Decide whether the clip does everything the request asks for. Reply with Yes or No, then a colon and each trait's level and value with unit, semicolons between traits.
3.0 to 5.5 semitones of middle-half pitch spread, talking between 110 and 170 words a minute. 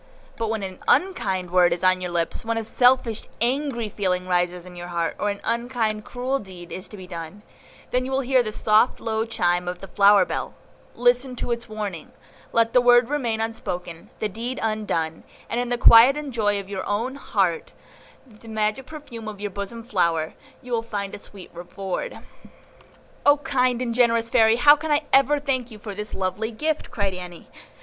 No: average, 4.6 semitones; average, 195 wpm